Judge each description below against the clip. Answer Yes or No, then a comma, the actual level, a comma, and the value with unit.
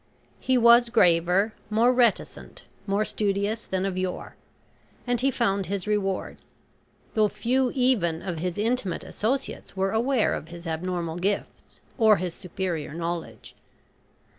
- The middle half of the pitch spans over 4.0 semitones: Yes, average, 4.5 semitones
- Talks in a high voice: Yes, high, 200 Hz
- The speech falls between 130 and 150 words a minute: Yes, slow, 135 wpm